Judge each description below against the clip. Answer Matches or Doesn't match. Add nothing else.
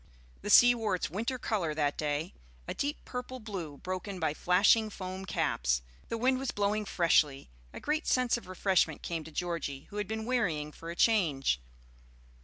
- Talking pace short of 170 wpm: Doesn't match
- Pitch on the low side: Doesn't match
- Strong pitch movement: Matches